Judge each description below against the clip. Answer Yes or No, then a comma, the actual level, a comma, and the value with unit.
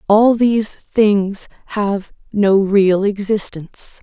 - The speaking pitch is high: Yes, high, 205 Hz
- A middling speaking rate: No, slow, 105 wpm